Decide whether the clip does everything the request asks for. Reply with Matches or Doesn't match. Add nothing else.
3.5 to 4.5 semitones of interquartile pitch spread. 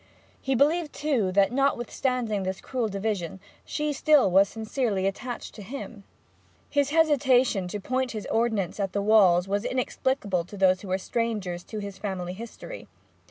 Doesn't match